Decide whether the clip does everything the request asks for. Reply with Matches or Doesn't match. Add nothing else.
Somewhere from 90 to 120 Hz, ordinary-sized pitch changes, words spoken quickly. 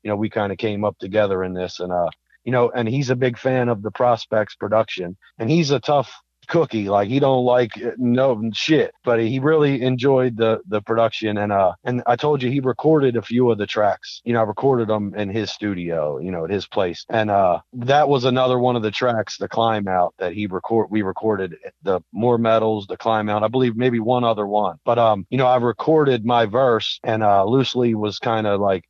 Matches